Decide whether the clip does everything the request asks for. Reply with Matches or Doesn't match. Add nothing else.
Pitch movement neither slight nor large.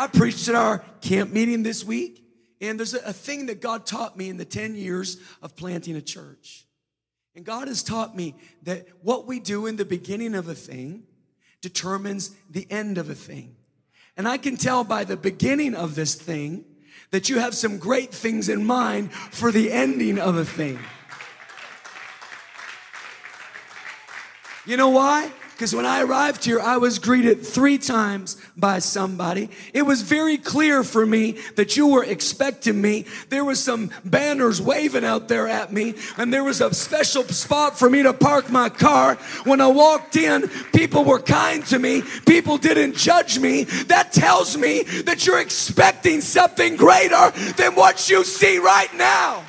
Doesn't match